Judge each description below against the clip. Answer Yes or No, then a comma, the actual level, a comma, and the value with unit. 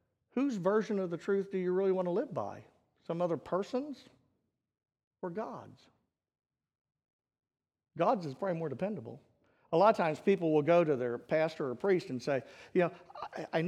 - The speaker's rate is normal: Yes, average, 180 wpm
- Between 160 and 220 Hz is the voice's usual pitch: Yes, medium, 185 Hz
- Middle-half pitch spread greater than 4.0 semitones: No, average, 3.2 semitones